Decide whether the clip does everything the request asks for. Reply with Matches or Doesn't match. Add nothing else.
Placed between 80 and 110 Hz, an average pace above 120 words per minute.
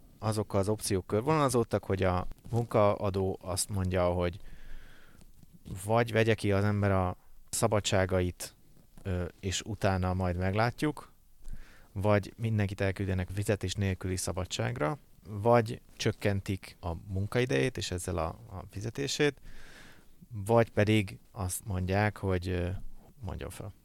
Doesn't match